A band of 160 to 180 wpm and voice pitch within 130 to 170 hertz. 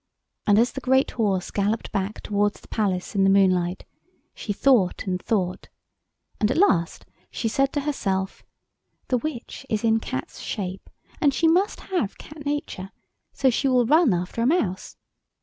No: average, 165 wpm; high, 220 Hz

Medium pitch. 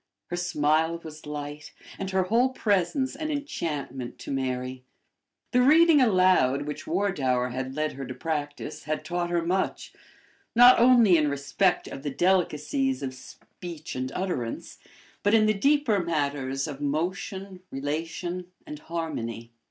Yes: medium, 165 Hz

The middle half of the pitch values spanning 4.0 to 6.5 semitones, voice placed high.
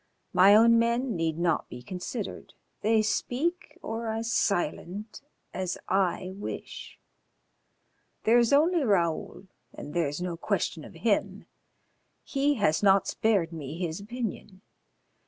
Yes: average, 4.9 semitones; high, 205 Hz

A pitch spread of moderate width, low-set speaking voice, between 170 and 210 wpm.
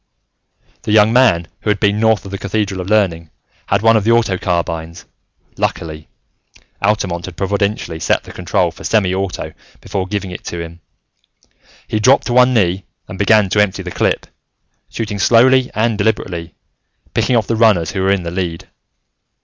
Yes: average, 3.6 semitones; low, 100 Hz; average, 175 wpm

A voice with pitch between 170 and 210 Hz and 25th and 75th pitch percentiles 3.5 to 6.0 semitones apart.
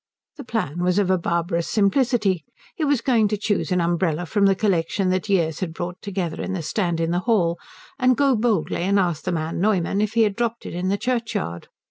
Yes: high, 190 Hz; average, 3.9 semitones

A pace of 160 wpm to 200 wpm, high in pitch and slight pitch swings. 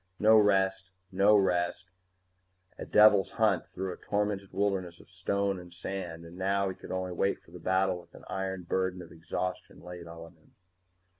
No: average, 175 wpm; very low, 95 Hz; narrow, 1.8 semitones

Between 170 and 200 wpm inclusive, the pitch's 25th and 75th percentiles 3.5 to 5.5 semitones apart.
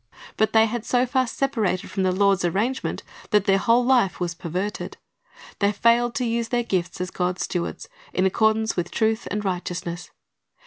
Yes: average, 175 wpm; average, 4.2 semitones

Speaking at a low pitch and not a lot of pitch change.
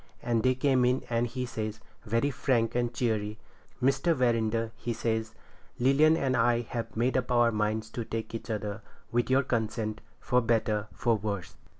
Yes: low, 115 Hz; narrow, 2.2 semitones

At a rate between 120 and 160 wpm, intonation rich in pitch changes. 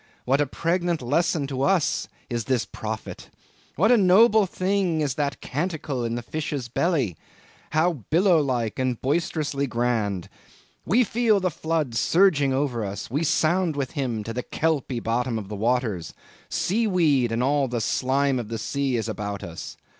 No: average, 170 wpm; wide, 5.8 semitones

